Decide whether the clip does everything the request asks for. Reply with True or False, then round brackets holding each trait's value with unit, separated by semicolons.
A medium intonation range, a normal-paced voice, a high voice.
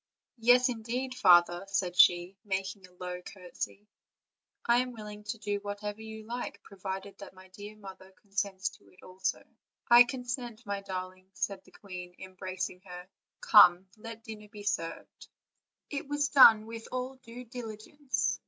True (3.7 semitones; 155 wpm; 205 Hz)